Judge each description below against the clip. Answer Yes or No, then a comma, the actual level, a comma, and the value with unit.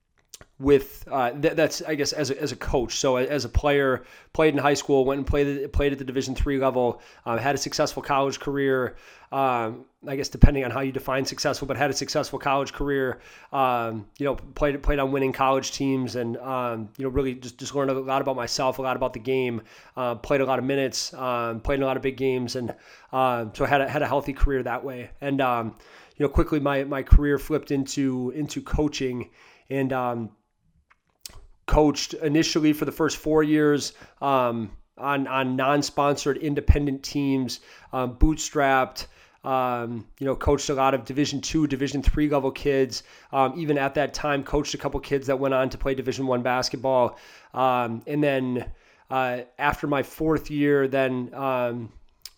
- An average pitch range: No, narrow, 2.0 semitones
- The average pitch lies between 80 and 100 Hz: No, low, 135 Hz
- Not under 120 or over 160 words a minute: No, average, 195 wpm